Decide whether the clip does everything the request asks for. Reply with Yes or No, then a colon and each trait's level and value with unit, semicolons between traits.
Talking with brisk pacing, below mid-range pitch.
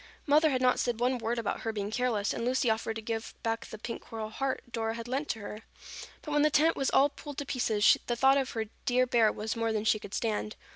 No: fast, 255 wpm; high, 230 Hz